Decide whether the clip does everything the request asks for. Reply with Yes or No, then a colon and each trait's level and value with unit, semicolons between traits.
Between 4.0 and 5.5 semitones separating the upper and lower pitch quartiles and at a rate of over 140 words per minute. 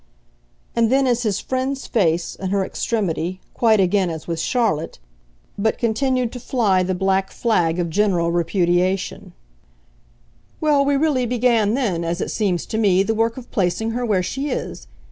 Yes: average, 5.1 semitones; average, 165 wpm